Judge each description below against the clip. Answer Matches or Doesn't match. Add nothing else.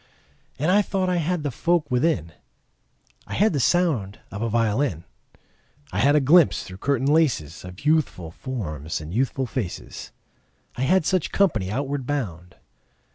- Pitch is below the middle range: Matches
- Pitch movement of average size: Doesn't match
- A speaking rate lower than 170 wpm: Matches